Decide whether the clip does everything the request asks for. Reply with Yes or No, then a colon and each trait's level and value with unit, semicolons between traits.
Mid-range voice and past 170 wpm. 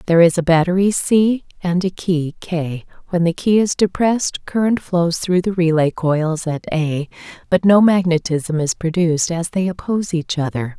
Yes: medium, 175 Hz; average, 180 wpm